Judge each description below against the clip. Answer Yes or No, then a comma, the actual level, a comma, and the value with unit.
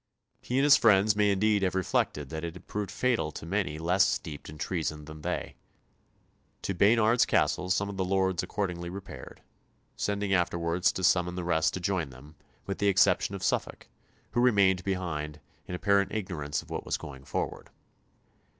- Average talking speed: Yes, average, 180 wpm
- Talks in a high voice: No, very low, 95 Hz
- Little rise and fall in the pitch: No, average, 3.3 semitones